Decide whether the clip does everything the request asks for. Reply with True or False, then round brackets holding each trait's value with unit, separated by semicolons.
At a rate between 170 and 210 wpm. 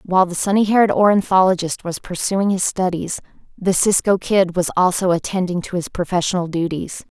False (160 wpm)